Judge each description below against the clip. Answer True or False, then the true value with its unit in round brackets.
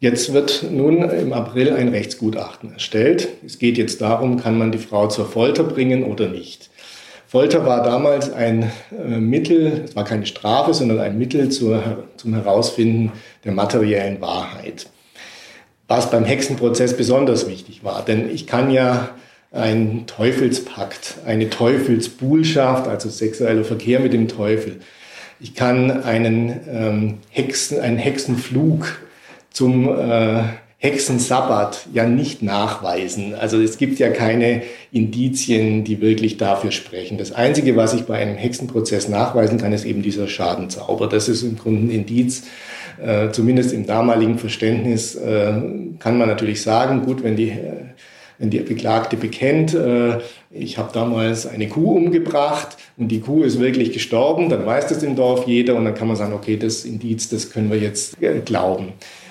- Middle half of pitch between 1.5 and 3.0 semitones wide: True (2.4 semitones)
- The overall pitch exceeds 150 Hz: False (115 Hz)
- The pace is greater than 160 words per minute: False (155 wpm)